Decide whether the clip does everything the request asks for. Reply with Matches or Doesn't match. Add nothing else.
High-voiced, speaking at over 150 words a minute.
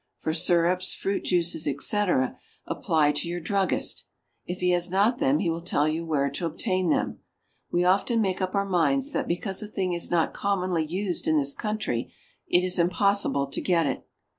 Doesn't match